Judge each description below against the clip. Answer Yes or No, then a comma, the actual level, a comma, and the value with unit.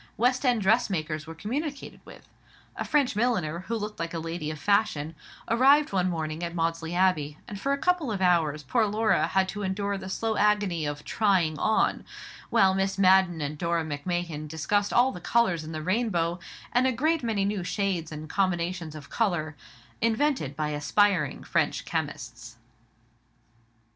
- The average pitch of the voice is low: No, medium, 185 Hz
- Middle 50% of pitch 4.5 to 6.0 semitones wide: Yes, average, 5.3 semitones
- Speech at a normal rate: Yes, average, 170 wpm